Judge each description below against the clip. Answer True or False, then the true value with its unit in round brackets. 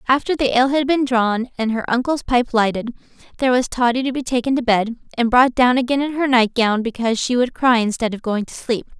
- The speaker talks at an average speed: False (240 wpm)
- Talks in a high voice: True (245 Hz)